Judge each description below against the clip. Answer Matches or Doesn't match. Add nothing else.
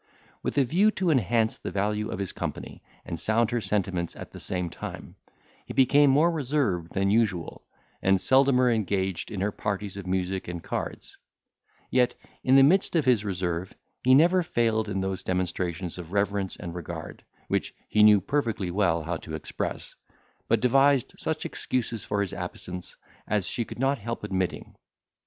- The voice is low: Matches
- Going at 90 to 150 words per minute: Doesn't match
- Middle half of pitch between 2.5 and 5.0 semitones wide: Doesn't match